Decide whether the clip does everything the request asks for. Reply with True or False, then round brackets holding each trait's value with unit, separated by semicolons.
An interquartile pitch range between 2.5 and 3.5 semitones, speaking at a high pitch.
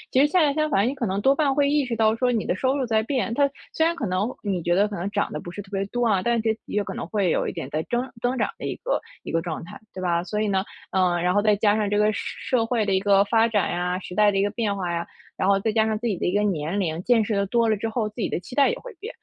False (3.9 semitones; 210 Hz)